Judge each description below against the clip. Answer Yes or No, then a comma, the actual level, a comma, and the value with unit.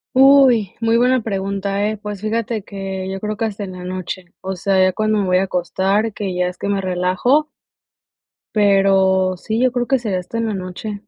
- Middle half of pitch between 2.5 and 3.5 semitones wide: Yes, average, 2.9 semitones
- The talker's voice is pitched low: No, high, 200 Hz